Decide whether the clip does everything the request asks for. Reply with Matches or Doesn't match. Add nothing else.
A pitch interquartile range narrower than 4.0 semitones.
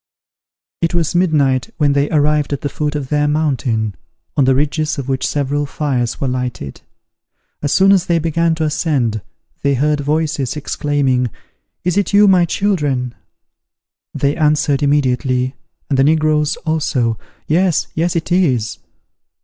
Matches